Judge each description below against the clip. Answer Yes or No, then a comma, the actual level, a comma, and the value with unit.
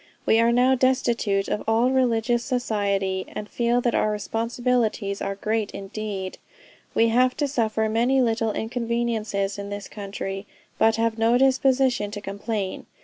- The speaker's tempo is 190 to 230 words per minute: No, average, 145 wpm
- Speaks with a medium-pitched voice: No, high, 225 Hz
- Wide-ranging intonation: No, average, 3.0 semitones